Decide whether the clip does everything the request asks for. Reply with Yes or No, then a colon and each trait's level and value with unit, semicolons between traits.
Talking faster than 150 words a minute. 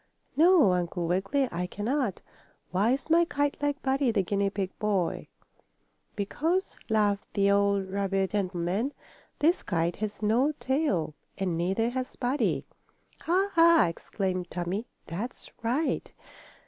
No: slow, 135 wpm